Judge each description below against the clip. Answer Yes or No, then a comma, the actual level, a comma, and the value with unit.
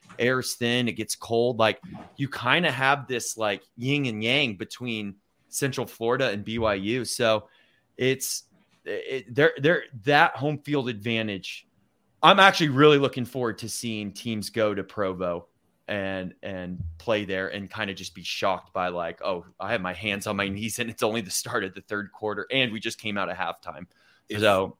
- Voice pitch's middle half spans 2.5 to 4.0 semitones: No, average, 4.4 semitones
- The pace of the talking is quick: No, average, 185 wpm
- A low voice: Yes, low, 115 Hz